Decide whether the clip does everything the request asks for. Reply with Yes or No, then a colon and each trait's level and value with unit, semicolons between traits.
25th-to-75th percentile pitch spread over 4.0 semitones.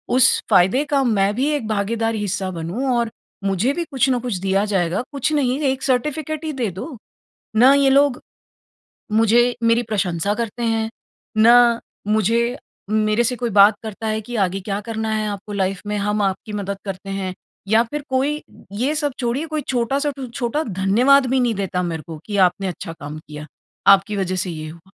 Yes: average, 4.5 semitones